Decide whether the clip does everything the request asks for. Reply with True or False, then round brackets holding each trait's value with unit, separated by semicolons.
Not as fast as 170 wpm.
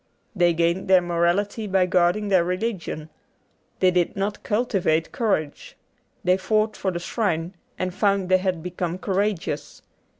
True (140 wpm)